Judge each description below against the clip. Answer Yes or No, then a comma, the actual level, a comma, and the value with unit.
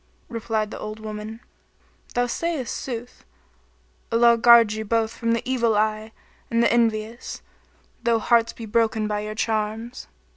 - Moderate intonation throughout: No, narrow, 1.6 semitones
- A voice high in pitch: Yes, high, 225 Hz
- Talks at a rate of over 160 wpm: No, average, 145 wpm